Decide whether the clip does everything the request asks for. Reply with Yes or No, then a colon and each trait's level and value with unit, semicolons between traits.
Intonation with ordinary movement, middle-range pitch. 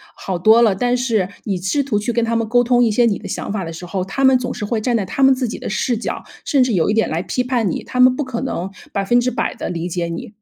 No: average, 4.4 semitones; high, 230 Hz